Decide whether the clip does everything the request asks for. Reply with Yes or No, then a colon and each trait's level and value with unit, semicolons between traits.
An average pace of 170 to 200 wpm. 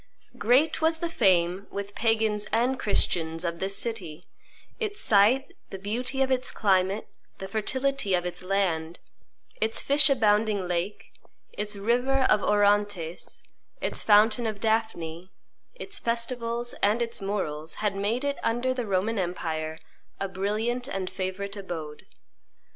No: slow, 135 wpm